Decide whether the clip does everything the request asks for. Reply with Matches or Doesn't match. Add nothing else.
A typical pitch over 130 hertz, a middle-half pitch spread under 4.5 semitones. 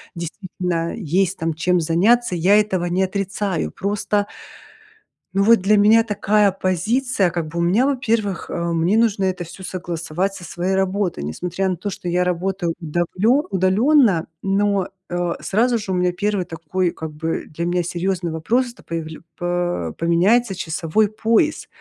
Matches